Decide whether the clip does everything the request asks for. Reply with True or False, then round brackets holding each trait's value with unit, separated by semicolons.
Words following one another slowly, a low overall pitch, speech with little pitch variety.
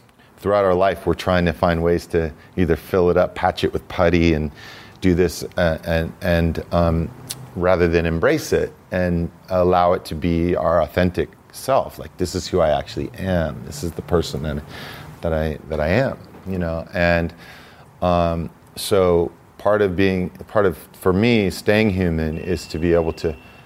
False (185 wpm; 85 Hz; 1.9 semitones)